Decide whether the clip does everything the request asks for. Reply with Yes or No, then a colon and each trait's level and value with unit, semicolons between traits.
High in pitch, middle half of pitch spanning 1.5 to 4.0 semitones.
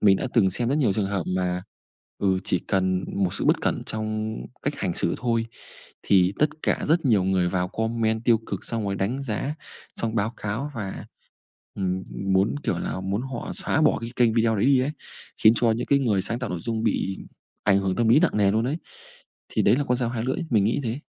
No: low, 110 Hz; average, 3.6 semitones